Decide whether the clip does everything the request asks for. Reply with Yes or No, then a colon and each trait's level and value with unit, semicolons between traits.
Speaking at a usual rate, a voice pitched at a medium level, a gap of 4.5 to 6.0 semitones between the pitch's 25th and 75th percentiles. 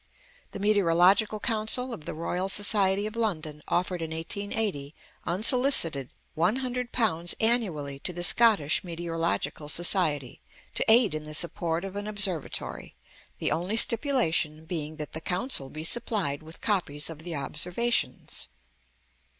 No: slow, 130 wpm; medium, 180 Hz; average, 5.2 semitones